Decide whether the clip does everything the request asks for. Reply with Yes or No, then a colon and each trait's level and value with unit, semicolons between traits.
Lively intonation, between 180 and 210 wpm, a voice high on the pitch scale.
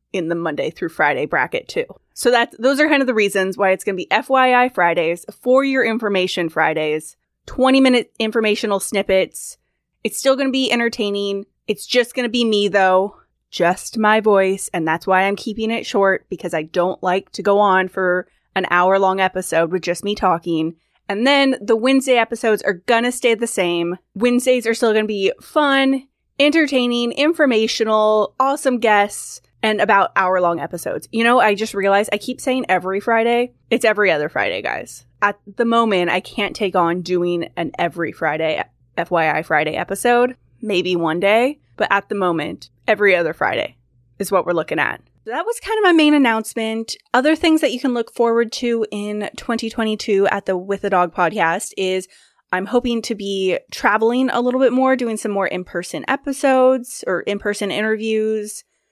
No: average, 4.7 semitones; average, 185 wpm; high, 210 Hz